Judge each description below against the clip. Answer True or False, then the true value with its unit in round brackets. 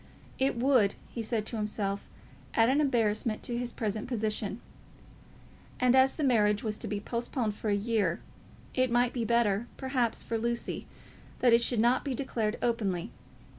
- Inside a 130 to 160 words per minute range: False (170 wpm)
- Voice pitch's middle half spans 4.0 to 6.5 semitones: False (2.7 semitones)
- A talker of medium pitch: False (230 Hz)